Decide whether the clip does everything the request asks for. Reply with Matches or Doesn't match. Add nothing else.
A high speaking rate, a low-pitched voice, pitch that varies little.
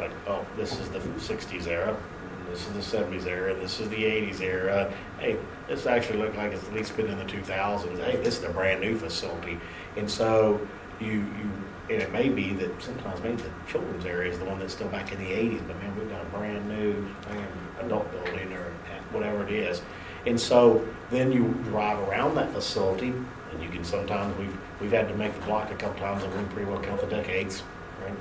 Matches